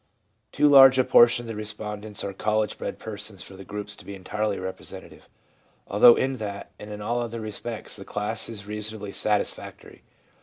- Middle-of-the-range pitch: No, low, 105 Hz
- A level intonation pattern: Yes, narrow, 1.9 semitones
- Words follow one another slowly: No, average, 180 wpm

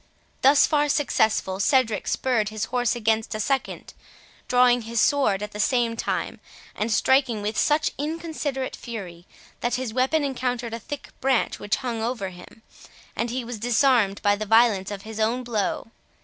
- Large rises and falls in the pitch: No, average, 3.3 semitones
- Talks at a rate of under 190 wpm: Yes, average, 165 wpm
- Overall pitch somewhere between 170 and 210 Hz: No, high, 235 Hz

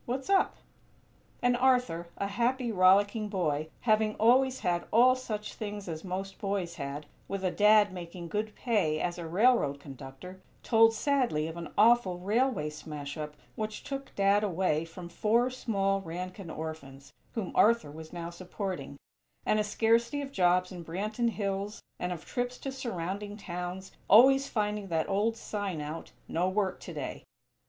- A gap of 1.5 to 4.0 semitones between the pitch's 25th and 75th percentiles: No, average, 4.7 semitones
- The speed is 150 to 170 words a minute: Yes, average, 160 wpm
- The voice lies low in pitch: No, high, 195 Hz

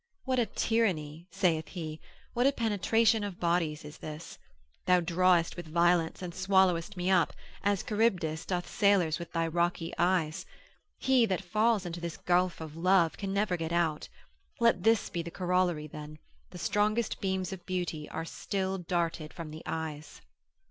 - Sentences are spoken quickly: No, average, 165 wpm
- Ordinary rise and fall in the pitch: Yes, average, 3.0 semitones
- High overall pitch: No, medium, 180 Hz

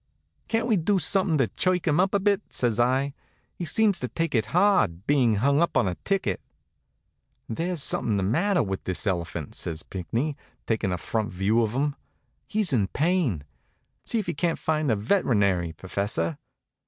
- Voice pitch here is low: Yes, low, 130 Hz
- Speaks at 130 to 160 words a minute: No, average, 180 wpm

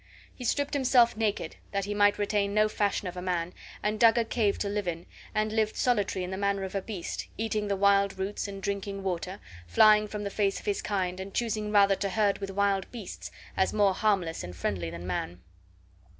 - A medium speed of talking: No, fast, 215 wpm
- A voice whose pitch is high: Yes, high, 200 Hz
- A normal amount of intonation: No, narrow, 2.0 semitones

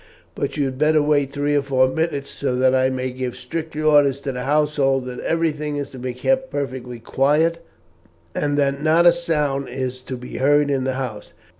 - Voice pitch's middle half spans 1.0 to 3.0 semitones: Yes, narrow, 2.5 semitones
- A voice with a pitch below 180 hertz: Yes, medium, 140 Hz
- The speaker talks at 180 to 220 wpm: Yes, average, 200 wpm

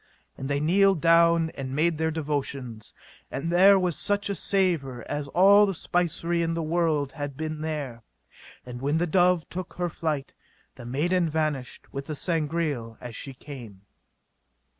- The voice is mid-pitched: Yes, medium, 155 Hz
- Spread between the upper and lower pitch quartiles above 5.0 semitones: No, average, 3.8 semitones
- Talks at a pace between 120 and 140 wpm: No, average, 165 wpm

